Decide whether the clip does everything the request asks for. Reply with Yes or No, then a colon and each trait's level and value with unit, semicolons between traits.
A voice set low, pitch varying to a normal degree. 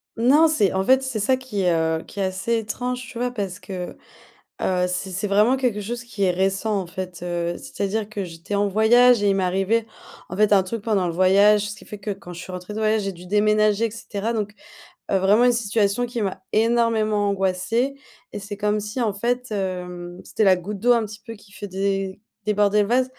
No: high, 205 Hz; average, 3.0 semitones